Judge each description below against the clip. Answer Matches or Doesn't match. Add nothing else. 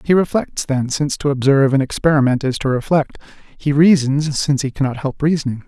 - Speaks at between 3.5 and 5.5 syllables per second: Doesn't match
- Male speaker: Matches